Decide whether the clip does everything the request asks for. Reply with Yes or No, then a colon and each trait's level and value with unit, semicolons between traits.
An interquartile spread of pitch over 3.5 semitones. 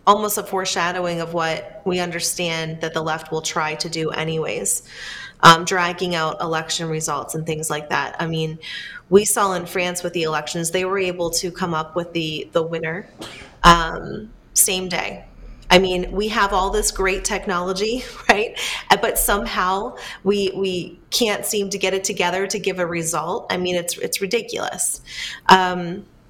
No: average, 2.9 semitones